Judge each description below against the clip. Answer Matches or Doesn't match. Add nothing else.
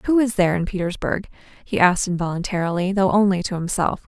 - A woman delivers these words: Matches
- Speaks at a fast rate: Doesn't match